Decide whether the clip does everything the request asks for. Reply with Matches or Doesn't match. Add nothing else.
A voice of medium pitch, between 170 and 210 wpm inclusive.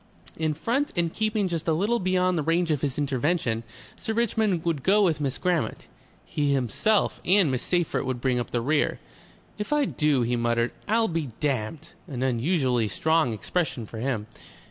Matches